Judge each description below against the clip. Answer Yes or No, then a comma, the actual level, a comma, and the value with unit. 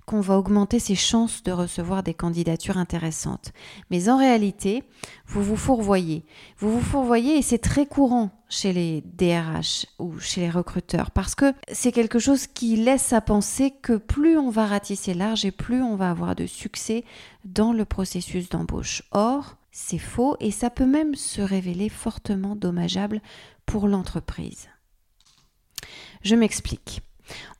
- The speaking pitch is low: No, high, 205 Hz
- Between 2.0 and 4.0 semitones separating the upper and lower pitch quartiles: No, average, 4.7 semitones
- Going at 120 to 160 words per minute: Yes, average, 155 wpm